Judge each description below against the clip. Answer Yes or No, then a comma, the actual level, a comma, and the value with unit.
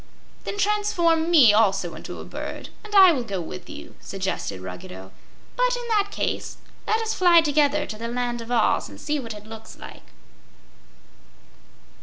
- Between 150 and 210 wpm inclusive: Yes, average, 170 wpm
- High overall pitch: Yes, very high, 280 Hz